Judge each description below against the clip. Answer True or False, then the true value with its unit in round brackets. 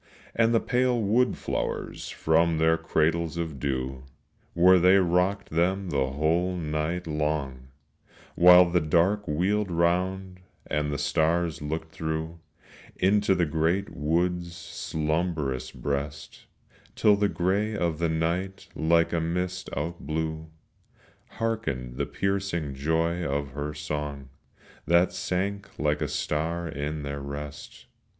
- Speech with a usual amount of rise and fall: True (3.3 semitones)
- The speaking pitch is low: True (85 Hz)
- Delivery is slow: True (125 wpm)